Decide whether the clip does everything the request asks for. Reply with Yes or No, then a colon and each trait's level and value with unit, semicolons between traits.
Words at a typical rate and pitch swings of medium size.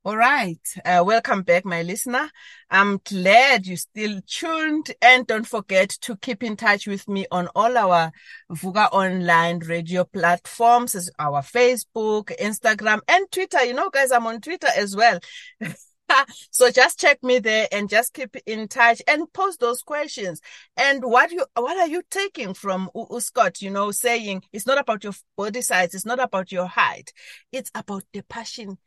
Yes: average, 170 wpm; average, 5.0 semitones